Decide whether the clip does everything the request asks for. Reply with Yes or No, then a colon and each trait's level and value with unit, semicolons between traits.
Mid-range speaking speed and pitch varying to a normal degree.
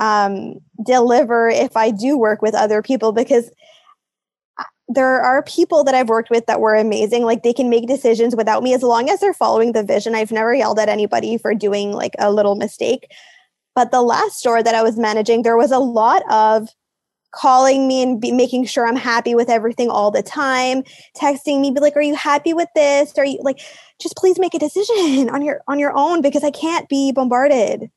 No: fast, 210 wpm; average, 4.1 semitones